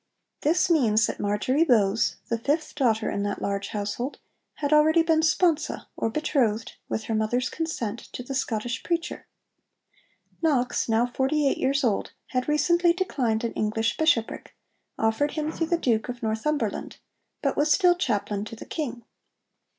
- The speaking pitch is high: Yes, very high, 250 Hz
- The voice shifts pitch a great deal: Yes, wide, 5.7 semitones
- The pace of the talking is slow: No, average, 160 wpm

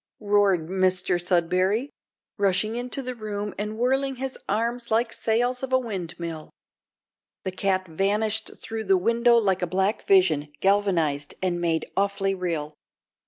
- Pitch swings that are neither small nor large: Yes, average, 4.0 semitones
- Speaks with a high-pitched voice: Yes, high, 195 Hz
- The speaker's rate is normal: Yes, average, 145 wpm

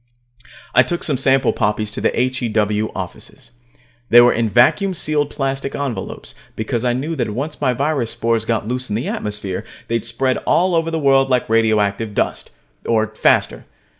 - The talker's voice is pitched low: Yes, low, 120 Hz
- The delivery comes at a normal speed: Yes, average, 170 wpm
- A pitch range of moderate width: Yes, average, 3.7 semitones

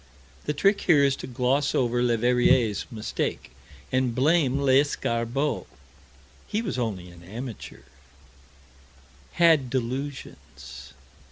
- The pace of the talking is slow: Yes, slow, 100 wpm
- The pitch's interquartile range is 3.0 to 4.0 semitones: Yes, average, 3.4 semitones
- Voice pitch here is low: Yes, low, 130 Hz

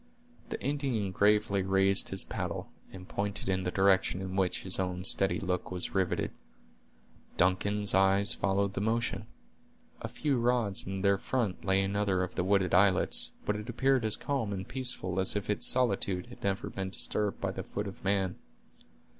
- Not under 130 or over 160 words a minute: No, average, 175 wpm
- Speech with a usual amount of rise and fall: No, narrow, 1.9 semitones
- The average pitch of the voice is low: Yes, low, 100 Hz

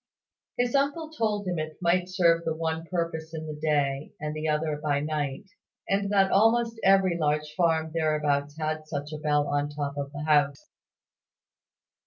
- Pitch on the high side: No, medium, 155 Hz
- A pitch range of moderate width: Yes, average, 3.5 semitones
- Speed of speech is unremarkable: Yes, average, 175 wpm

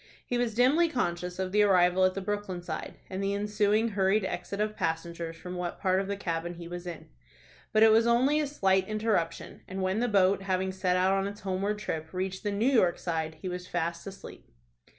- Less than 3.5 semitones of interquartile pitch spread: Yes, average, 2.8 semitones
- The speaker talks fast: Yes, fast, 220 wpm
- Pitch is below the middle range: No, high, 190 Hz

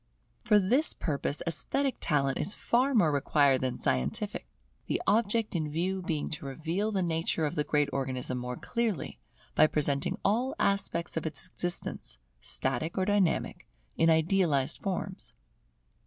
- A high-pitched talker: No, medium, 165 Hz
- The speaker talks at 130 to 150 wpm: Yes, average, 145 wpm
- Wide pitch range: Yes, wide, 5.7 semitones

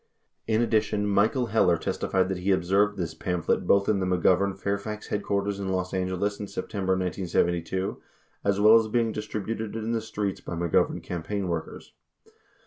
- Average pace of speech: Yes, average, 175 wpm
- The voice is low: Yes, low, 100 Hz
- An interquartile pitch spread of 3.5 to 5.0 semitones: No, narrow, 2.4 semitones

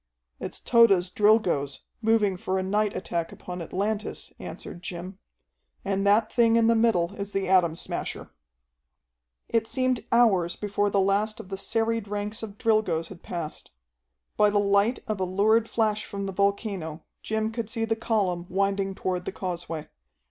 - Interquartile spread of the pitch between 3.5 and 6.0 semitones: No, average, 3.1 semitones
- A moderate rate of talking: Yes, average, 165 wpm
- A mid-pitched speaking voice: No, high, 200 Hz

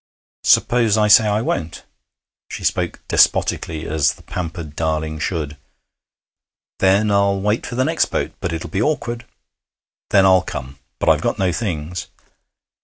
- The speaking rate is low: No, average, 150 wpm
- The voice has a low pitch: Yes, very low, 95 Hz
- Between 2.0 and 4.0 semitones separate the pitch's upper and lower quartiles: No, average, 5.0 semitones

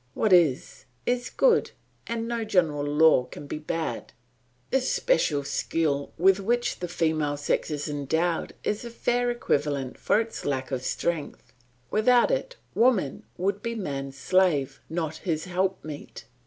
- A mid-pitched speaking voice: Yes, medium, 170 Hz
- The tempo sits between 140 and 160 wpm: Yes, average, 145 wpm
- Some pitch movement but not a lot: No, wide, 7.3 semitones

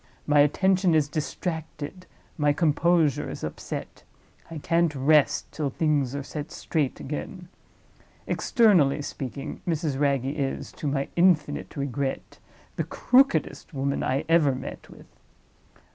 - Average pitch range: Yes, average, 3.2 semitones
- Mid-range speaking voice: Yes, medium, 150 Hz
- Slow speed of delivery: Yes, slow, 125 wpm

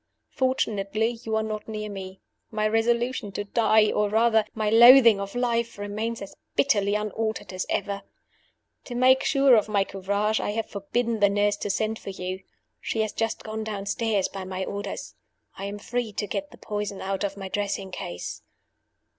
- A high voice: Yes, high, 210 Hz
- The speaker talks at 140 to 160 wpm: No, average, 180 wpm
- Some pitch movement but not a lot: No, narrow, 2.1 semitones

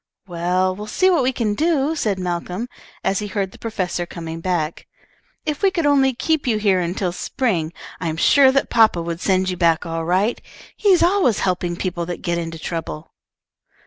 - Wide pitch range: Yes, wide, 6.8 semitones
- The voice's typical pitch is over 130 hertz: Yes, medium, 185 Hz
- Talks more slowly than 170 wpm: No, average, 190 wpm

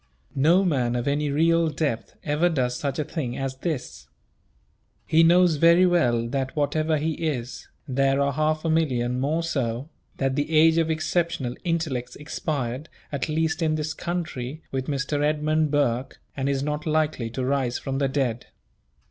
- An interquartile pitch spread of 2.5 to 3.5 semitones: Yes, average, 3.2 semitones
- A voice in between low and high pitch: Yes, medium, 145 Hz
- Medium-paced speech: Yes, average, 165 wpm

